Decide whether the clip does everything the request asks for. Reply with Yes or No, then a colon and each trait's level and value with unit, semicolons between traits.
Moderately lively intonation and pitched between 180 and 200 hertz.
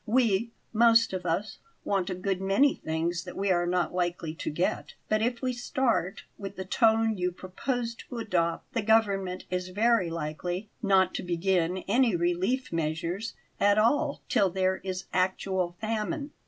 Yes: average, 4.0 semitones; high, 190 Hz